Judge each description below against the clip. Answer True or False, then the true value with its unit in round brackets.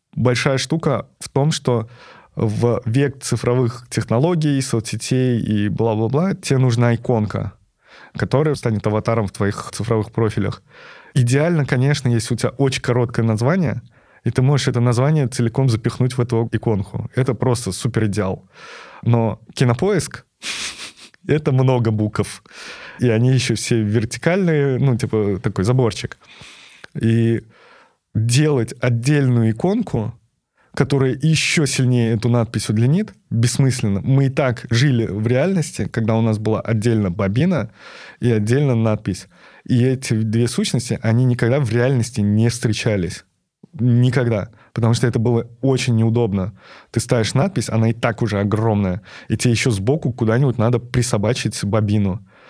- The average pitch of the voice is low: True (120 Hz)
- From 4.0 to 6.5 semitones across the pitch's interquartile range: False (2.9 semitones)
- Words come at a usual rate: True (135 wpm)